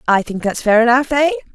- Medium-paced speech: Yes, average, 195 wpm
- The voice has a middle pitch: No, very high, 250 Hz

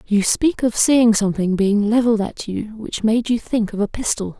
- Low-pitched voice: No, high, 220 Hz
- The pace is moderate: No, fast, 220 wpm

